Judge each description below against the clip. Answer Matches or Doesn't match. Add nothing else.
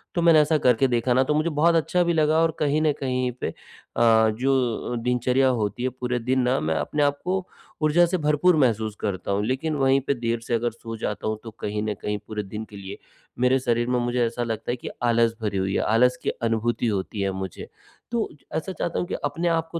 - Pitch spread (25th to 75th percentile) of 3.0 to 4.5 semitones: Doesn't match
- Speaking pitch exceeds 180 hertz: Doesn't match